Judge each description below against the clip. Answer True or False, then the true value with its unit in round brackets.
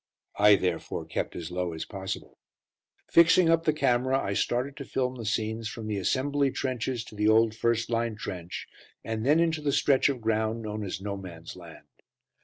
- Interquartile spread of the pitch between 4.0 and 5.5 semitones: True (4.6 semitones)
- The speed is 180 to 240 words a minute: True (190 wpm)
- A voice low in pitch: True (115 Hz)